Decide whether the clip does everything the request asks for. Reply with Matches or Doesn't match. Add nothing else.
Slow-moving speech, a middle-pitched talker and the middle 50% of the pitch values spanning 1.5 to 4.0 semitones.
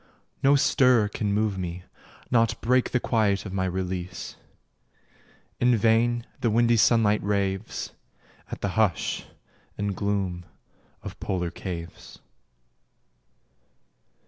Doesn't match